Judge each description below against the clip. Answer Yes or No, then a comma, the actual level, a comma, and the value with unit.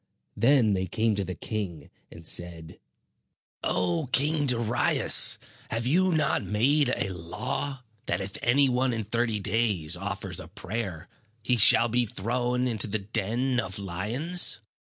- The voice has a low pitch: Yes, low, 115 Hz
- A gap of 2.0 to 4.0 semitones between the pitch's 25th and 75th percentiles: No, average, 4.6 semitones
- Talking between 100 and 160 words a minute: Yes, average, 145 wpm